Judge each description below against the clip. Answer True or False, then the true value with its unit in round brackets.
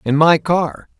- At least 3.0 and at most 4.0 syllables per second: True (3.7 syllables/s)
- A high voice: False (150 Hz)